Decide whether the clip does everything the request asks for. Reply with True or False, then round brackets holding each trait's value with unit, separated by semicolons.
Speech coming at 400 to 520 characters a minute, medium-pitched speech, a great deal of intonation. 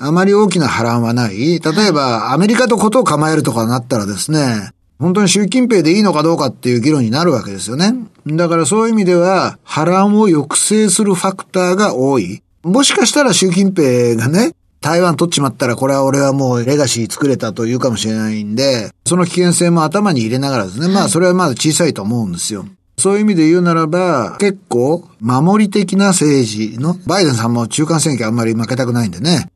True (430 characters per minute; 155 Hz; 7.4 semitones)